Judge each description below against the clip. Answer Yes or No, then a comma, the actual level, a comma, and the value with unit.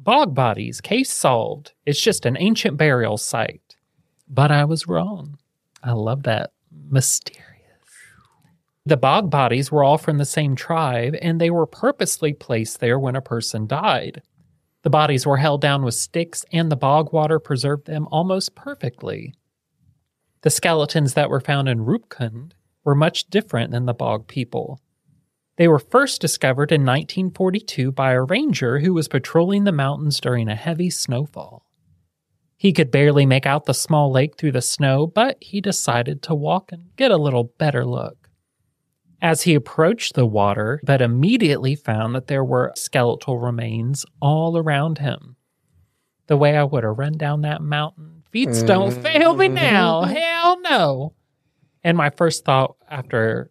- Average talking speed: Yes, average, 160 wpm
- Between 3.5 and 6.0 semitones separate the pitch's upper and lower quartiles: Yes, average, 3.8 semitones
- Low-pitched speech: No, medium, 150 Hz